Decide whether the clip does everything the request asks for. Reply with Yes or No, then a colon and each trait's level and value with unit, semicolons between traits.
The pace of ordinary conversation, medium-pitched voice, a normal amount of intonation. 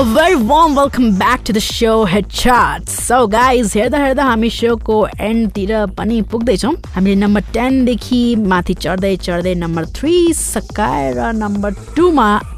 No: average, 155 wpm; high, 225 Hz; average, 3.6 semitones